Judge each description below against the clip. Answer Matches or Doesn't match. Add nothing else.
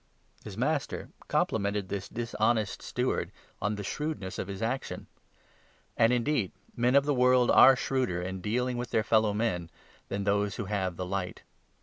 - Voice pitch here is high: Doesn't match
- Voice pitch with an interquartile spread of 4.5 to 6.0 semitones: Doesn't match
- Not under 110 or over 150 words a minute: Doesn't match